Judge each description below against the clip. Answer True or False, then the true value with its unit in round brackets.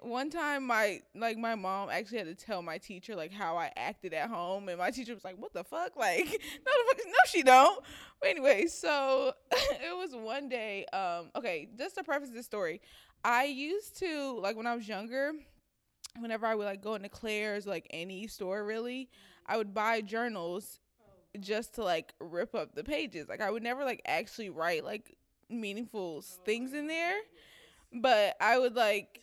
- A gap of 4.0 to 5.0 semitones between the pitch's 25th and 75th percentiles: False (5.4 semitones)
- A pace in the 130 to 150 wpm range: False (195 wpm)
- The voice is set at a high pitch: True (230 Hz)